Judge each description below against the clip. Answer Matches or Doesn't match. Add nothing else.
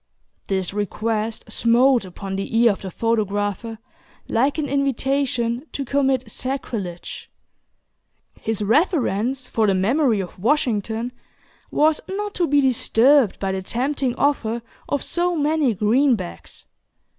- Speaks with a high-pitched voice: Matches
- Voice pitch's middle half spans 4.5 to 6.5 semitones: Matches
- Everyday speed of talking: Doesn't match